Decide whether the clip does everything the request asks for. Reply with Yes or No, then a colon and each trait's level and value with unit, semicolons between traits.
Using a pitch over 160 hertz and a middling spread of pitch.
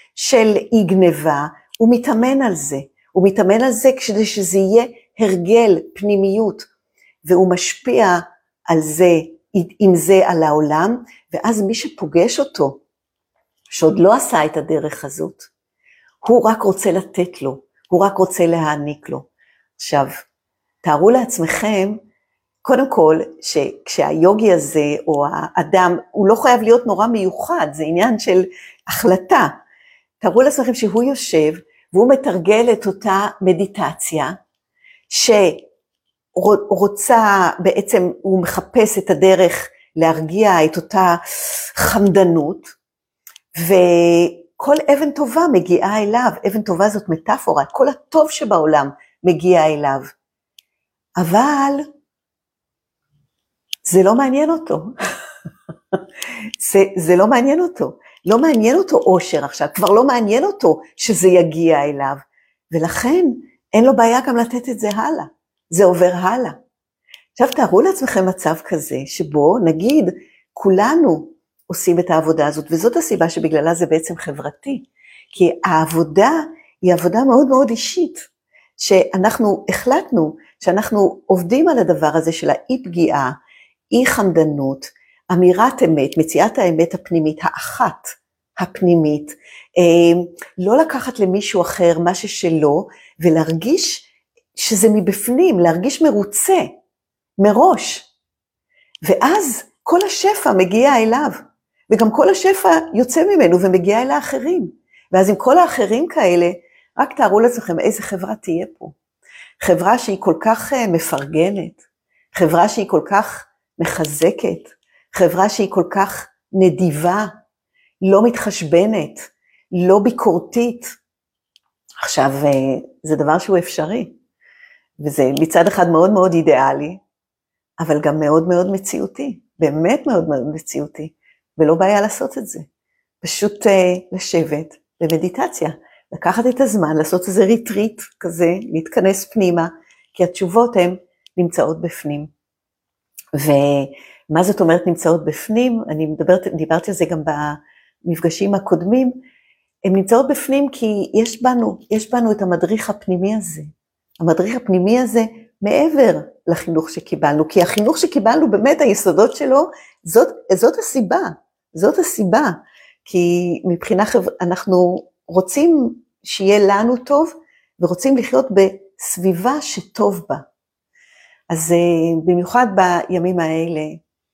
No: high, 190 Hz; wide, 5.9 semitones